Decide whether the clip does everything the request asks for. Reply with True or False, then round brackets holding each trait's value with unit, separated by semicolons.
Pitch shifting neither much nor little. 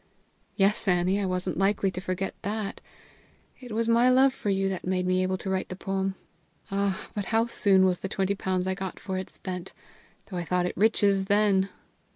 False (1.6 semitones)